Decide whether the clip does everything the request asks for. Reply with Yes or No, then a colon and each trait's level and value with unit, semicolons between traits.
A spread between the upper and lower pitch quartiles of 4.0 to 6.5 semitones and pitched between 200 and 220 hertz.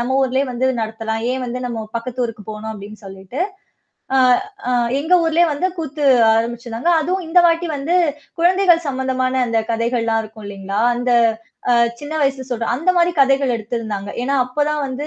No: average, 4.5 semitones; very high, 255 Hz